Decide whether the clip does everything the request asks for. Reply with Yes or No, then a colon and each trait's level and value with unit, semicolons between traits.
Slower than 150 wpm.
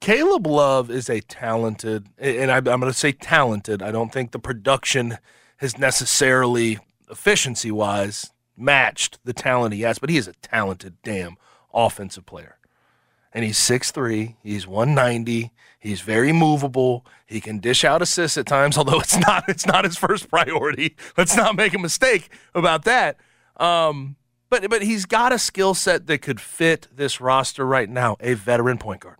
No: average, 165 wpm